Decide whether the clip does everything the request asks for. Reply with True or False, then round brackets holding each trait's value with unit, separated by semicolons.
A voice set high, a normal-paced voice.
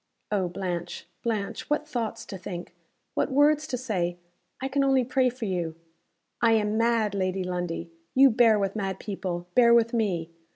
True (215 Hz; 170 wpm)